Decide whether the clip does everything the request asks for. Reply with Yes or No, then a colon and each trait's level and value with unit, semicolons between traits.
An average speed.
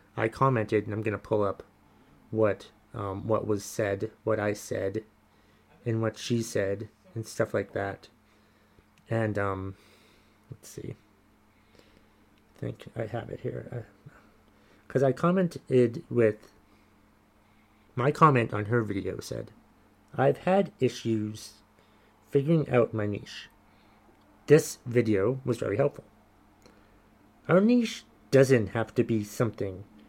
No: slow, 130 wpm